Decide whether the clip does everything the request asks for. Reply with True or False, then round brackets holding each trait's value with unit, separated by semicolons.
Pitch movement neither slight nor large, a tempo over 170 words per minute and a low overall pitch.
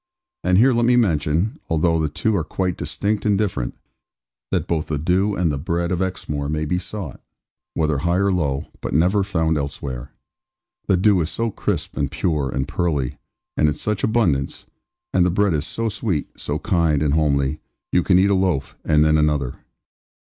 True (4.4 semitones; 190 wpm; 85 Hz)